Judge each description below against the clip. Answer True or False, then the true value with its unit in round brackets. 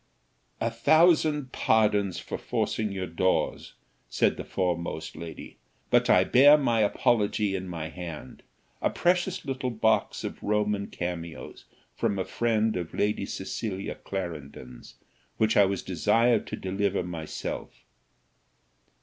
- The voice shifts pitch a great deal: False (4.4 semitones)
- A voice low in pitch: True (100 Hz)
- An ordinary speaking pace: False (125 wpm)